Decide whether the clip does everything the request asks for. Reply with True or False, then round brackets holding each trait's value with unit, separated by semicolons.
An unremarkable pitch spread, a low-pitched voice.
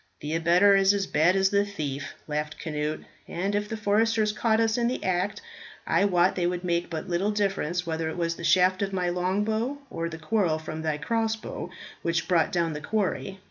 False (3.7 semitones; 180 Hz)